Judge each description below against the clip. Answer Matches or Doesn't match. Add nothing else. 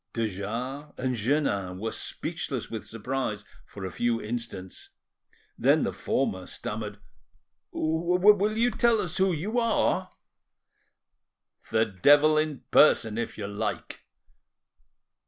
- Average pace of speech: Doesn't match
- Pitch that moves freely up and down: Matches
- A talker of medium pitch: Doesn't match